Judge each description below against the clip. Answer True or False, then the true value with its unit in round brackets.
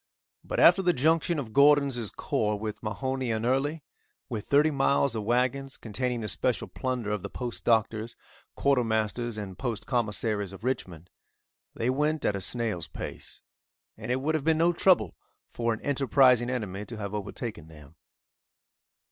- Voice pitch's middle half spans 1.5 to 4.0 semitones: False (4.4 semitones)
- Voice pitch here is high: False (120 Hz)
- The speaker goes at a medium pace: True (160 wpm)